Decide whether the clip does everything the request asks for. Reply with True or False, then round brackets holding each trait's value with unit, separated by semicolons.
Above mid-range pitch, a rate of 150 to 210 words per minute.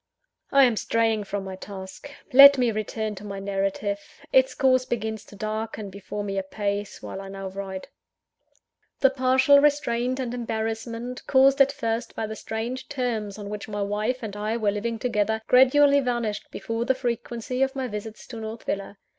True (225 Hz; 175 wpm)